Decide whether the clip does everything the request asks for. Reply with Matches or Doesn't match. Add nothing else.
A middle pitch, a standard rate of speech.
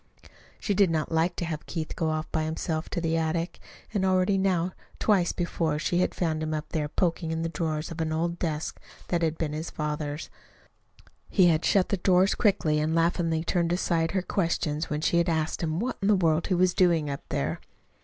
Doesn't match